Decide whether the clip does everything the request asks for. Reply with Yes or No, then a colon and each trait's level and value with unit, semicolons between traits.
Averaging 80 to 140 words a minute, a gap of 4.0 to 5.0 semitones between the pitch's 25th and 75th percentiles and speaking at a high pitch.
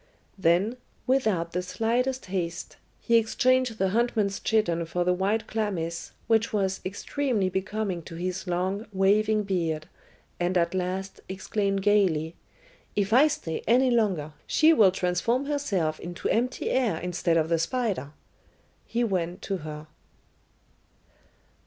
Yes: slow, 135 wpm; average, 4.3 semitones; high, 195 Hz